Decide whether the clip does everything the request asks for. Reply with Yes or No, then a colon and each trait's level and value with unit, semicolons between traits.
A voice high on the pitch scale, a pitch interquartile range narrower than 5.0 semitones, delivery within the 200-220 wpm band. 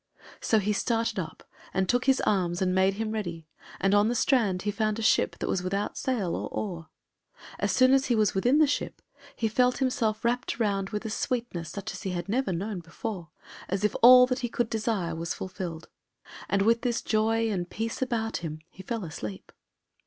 Yes: high, 215 Hz; average, 3.9 semitones; fast, 205 wpm